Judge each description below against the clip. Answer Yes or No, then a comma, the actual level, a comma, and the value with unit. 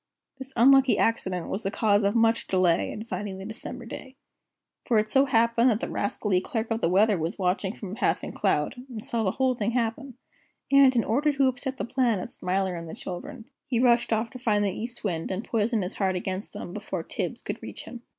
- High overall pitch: Yes, high, 225 Hz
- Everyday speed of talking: No, fast, 225 wpm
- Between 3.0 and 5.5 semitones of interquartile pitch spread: Yes, average, 4.2 semitones